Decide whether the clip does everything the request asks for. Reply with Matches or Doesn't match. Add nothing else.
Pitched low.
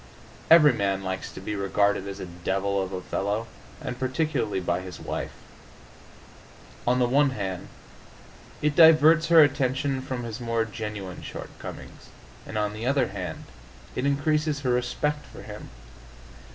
Matches